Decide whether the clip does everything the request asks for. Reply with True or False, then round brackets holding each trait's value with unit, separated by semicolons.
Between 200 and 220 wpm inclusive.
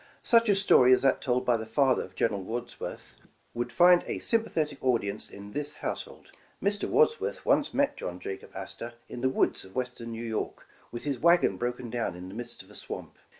True (205 wpm)